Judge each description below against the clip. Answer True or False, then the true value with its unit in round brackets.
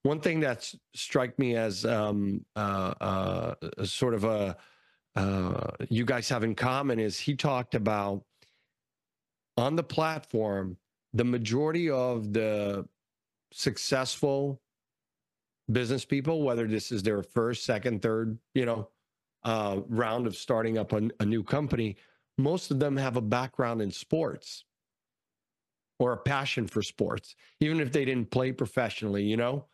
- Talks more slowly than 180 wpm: True (145 wpm)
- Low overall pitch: True (115 Hz)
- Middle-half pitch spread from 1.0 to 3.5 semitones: False (3.9 semitones)